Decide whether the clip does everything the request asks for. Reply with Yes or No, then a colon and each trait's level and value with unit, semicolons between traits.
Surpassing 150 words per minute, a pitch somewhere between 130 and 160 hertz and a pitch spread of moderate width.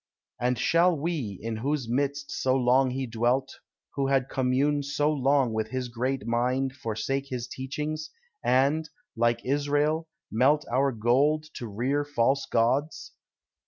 No: average, 140 wpm; low, 135 Hz; average, 3.0 semitones